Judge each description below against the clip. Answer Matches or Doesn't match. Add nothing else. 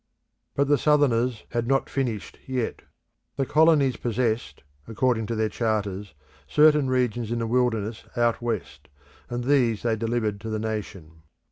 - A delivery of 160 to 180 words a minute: Doesn't match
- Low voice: Matches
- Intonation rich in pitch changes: Doesn't match